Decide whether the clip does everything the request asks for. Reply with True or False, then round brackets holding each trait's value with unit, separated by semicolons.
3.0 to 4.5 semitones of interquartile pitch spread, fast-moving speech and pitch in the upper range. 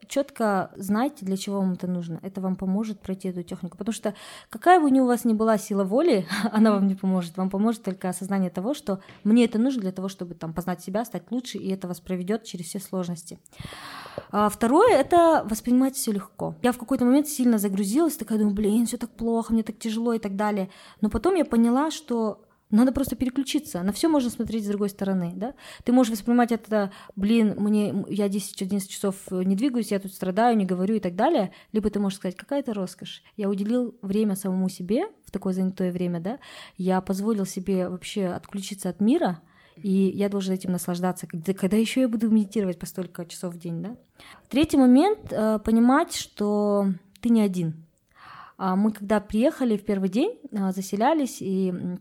True (3.6 semitones; 190 wpm; 205 Hz)